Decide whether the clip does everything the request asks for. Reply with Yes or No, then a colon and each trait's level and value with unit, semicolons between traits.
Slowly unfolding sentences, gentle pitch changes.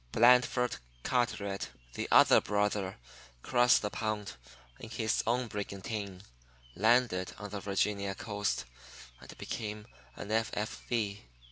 Yes: slow, 110 wpm; narrow, 2.2 semitones